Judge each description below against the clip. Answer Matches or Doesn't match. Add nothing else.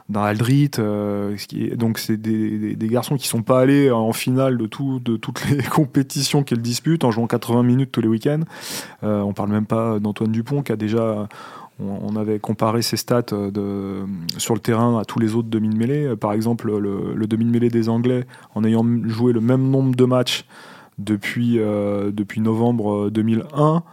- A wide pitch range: Doesn't match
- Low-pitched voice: Matches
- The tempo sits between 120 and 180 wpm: Doesn't match